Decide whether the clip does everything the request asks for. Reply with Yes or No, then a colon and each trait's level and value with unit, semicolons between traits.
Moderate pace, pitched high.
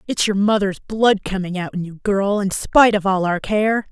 No: fast, 230 wpm; high, 200 Hz